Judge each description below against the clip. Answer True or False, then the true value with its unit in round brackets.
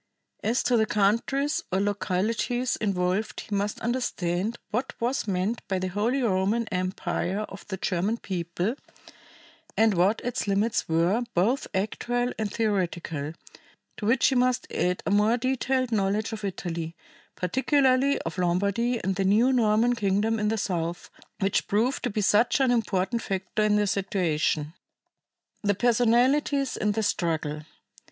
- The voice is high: True (210 Hz)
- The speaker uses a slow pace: False (145 wpm)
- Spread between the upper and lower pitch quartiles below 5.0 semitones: True (4.1 semitones)